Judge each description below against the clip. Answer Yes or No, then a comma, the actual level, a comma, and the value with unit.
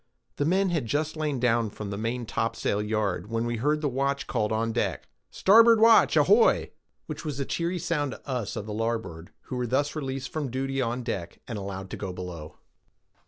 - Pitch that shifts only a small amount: No, average, 5.3 semitones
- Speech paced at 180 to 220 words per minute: Yes, average, 190 wpm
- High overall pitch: No, low, 120 Hz